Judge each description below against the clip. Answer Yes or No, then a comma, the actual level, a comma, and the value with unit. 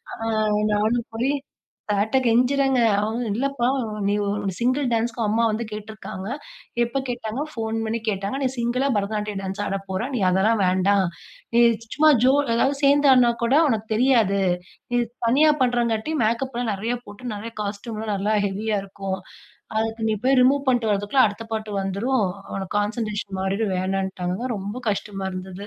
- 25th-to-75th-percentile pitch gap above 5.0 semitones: No, average, 3.4 semitones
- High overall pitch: Yes, high, 220 Hz